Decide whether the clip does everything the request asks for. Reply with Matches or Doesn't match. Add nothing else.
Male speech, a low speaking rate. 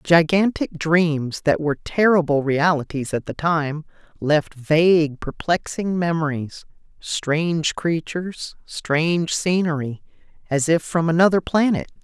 Doesn't match